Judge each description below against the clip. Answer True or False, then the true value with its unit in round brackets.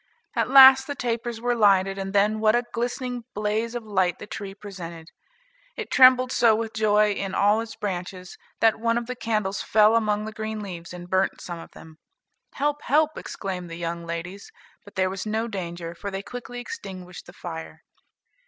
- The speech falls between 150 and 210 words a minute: True (190 wpm)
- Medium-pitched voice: False (210 Hz)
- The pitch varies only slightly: False (3.8 semitones)